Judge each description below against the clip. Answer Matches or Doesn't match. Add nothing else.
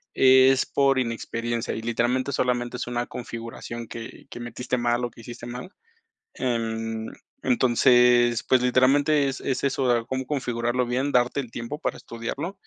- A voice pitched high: Doesn't match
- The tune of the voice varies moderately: Doesn't match